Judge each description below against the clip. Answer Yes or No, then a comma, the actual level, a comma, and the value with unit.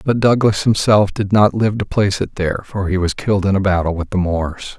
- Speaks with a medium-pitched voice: No, low, 100 Hz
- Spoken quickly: Yes, fast, 250 wpm